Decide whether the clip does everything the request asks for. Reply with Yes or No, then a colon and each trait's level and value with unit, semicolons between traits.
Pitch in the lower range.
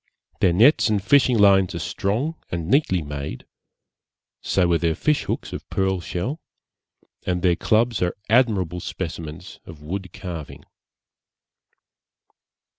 Yes: very low, 95 Hz